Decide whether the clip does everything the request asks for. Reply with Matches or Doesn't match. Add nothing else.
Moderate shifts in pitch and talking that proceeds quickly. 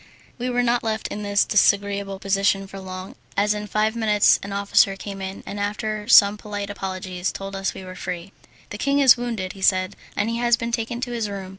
Doesn't match